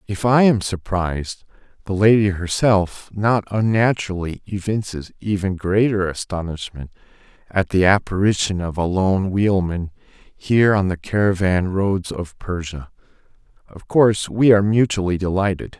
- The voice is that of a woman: No, male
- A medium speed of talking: No, slow, 125 wpm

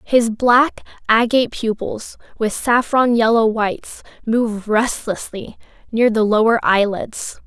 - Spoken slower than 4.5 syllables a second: Yes, 4.0 syllables/s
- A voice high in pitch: Yes, high, 225 Hz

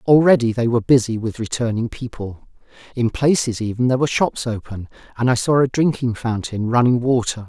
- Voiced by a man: Yes, male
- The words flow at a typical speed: Yes, average, 175 wpm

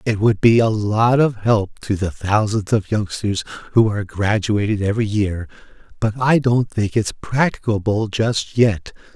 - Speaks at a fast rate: No, average, 155 wpm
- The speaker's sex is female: No, male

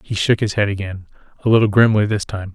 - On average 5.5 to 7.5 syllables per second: Yes, 6.1 syllables/s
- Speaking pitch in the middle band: No, low, 105 Hz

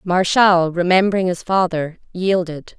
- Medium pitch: Yes, medium, 180 Hz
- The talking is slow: Yes, slow, 110 wpm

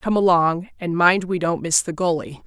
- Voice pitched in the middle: Yes, medium, 175 Hz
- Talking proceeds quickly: Yes, fast, 220 wpm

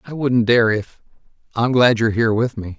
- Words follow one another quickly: Yes, fast, 215 wpm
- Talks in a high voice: No, low, 115 Hz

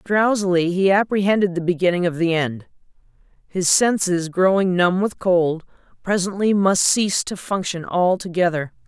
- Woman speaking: Yes, female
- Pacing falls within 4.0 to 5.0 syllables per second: Yes, 4.8 syllables/s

